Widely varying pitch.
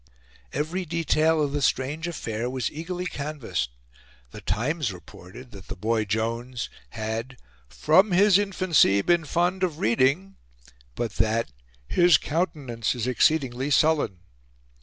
Yes: wide, 6.3 semitones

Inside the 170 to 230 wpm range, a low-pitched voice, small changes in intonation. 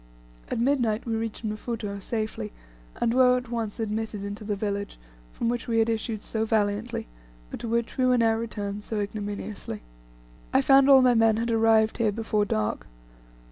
No: average, 180 wpm; high, 225 Hz; narrow, 2.0 semitones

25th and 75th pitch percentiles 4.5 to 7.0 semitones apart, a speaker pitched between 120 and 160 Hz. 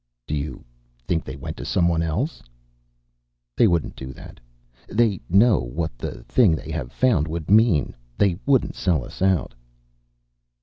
No: wide, 5.5 semitones; very low, 85 Hz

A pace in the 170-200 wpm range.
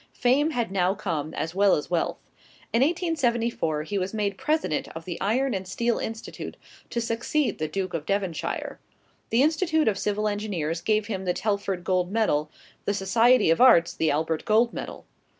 Yes: average, 175 wpm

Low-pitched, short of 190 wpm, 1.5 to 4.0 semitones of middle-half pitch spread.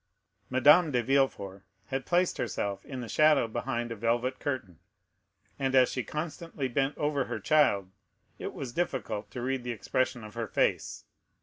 Yes: low, 130 Hz; average, 165 wpm; average, 3.4 semitones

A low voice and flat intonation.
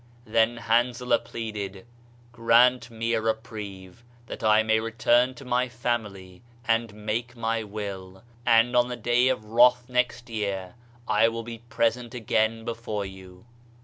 Yes: low, 115 Hz; narrow, 2.1 semitones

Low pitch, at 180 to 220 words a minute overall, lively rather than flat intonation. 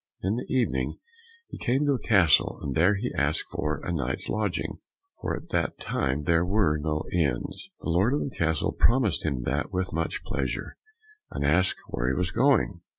Yes: very low, 85 Hz; average, 190 wpm; wide, 6.1 semitones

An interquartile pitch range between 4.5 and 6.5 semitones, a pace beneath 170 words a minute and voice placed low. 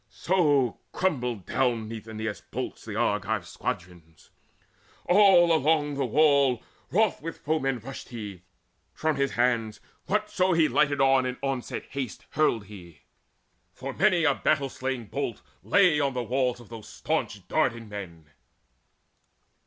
Yes: wide, 5.4 semitones; average, 140 wpm; low, 130 Hz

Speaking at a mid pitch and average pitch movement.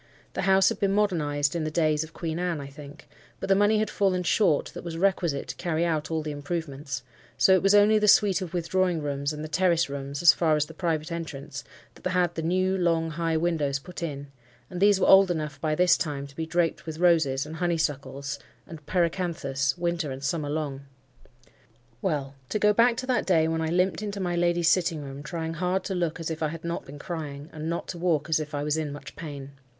Yes: medium, 165 Hz; average, 3.2 semitones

